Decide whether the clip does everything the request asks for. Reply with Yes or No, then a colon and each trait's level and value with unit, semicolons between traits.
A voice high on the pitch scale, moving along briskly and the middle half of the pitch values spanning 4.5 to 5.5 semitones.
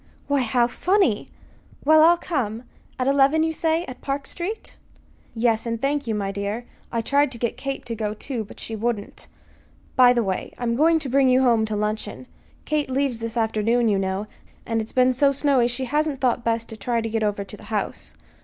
No: high, 240 Hz; fast, 210 wpm; average, 3.9 semitones